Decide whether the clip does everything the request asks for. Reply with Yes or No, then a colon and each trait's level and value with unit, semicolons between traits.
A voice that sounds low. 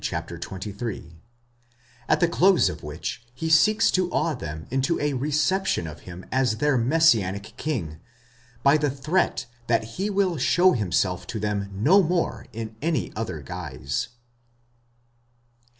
Yes: low, 130 Hz